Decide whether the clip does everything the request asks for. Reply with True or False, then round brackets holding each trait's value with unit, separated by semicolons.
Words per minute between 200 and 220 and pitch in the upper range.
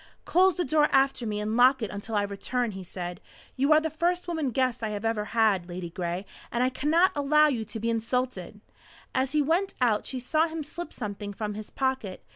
True (205 wpm; 245 Hz)